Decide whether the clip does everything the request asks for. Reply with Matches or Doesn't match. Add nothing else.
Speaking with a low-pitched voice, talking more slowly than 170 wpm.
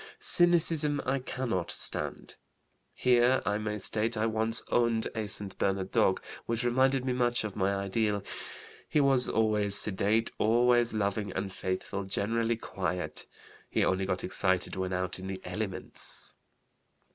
Matches